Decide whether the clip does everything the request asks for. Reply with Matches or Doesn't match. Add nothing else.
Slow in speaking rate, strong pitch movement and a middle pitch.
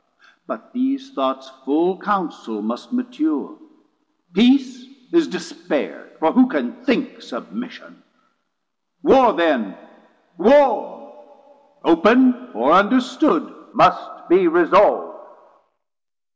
Doesn't match